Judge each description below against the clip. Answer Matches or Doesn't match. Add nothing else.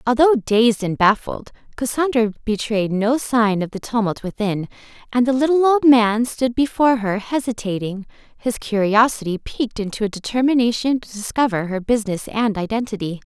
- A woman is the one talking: Matches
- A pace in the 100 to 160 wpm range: Matches